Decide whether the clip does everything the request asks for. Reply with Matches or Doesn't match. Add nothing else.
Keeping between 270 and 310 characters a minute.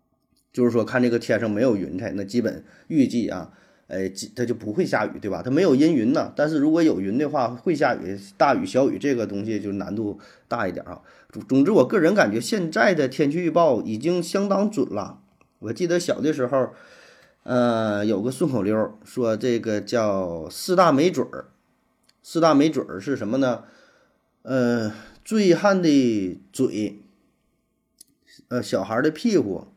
Doesn't match